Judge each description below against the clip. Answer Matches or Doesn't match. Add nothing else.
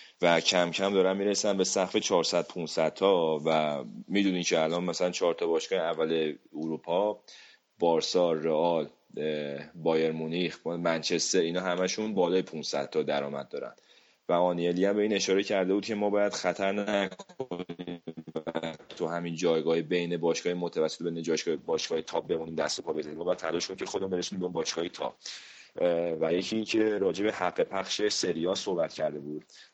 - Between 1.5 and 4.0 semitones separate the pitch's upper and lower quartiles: Matches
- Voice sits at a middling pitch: Doesn't match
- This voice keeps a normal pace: Doesn't match